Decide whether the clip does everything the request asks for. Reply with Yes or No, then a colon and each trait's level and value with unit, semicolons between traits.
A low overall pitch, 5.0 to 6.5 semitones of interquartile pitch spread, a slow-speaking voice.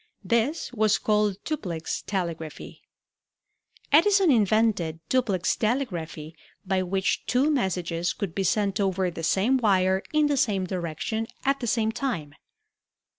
No: high, 200 Hz; average, 5.3 semitones; slow, 125 wpm